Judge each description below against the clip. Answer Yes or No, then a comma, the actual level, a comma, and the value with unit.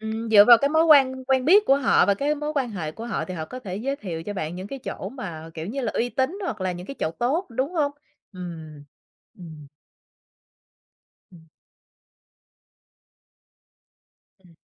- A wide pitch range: Yes, wide, 7.4 semitones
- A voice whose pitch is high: Yes, high, 225 Hz